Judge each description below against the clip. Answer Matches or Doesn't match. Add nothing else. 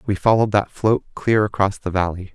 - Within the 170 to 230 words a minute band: Matches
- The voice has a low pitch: Matches